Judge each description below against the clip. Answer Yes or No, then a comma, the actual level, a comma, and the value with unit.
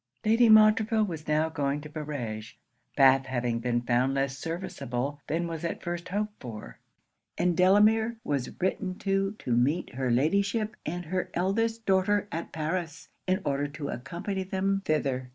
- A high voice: No, medium, 165 Hz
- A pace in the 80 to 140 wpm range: No, average, 155 wpm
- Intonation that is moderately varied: No, wide, 6.2 semitones